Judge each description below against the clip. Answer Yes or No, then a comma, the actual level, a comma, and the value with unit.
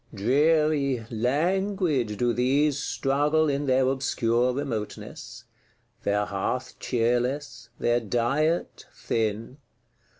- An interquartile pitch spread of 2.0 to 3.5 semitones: No, average, 3.9 semitones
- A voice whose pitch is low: Yes, low, 130 Hz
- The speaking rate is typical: No, slow, 90 wpm